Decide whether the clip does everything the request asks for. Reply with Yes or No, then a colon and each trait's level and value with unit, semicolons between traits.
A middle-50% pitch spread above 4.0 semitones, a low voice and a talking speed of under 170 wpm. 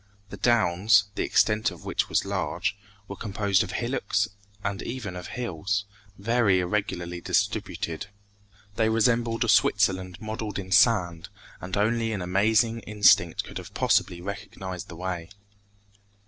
No: average, 3.4 semitones; low, 100 Hz; slow, 135 wpm